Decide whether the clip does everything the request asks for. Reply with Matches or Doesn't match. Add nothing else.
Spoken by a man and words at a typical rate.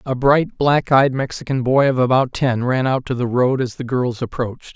Doesn't match